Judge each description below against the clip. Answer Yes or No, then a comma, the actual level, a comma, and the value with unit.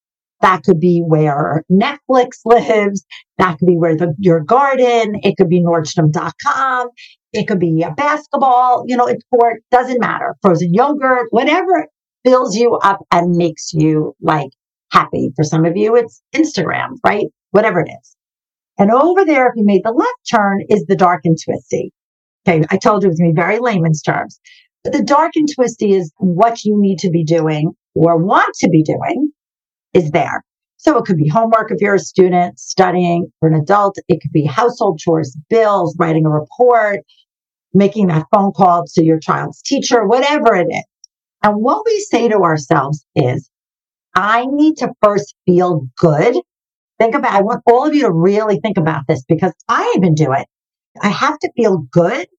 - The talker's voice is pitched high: Yes, high, 195 Hz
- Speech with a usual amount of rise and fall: No, wide, 6.3 semitones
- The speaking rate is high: No, average, 185 wpm